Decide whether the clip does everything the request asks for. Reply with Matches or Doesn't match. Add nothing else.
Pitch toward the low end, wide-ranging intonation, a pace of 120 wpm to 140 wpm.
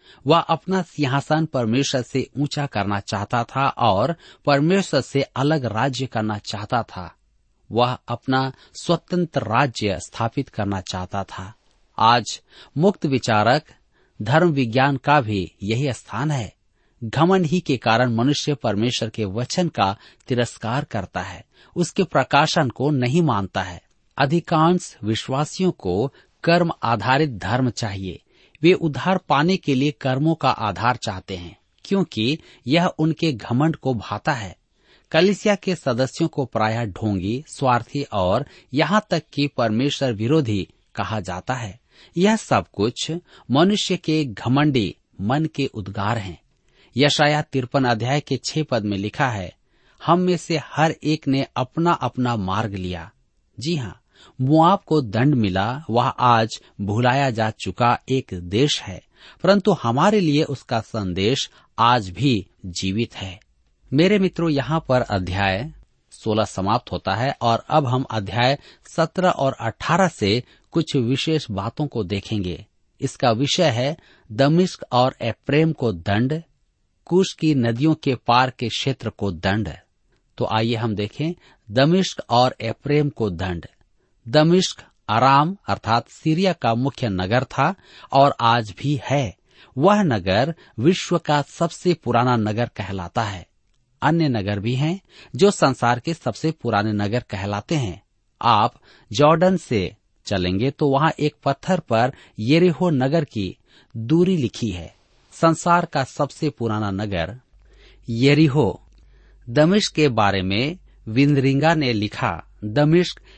Matches